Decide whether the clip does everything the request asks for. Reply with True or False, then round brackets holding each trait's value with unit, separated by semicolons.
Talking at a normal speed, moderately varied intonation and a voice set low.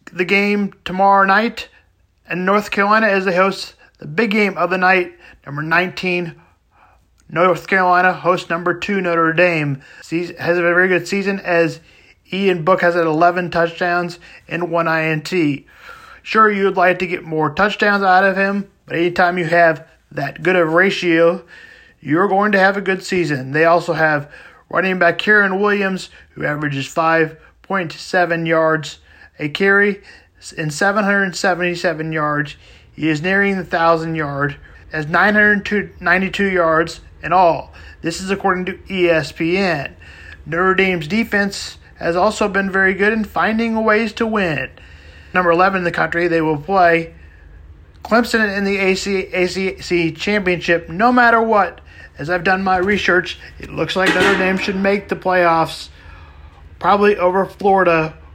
False (150 wpm; 3.1 semitones; 180 Hz)